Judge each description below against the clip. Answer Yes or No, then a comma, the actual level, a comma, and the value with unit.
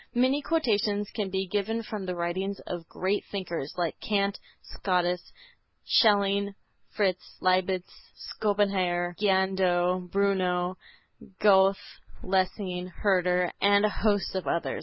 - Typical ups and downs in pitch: No, narrow, 2.1 semitones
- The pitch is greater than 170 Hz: Yes, high, 190 Hz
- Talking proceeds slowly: Yes, slow, 115 wpm